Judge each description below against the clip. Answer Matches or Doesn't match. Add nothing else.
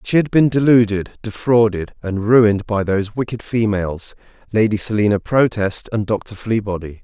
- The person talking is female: Doesn't match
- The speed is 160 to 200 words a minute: Doesn't match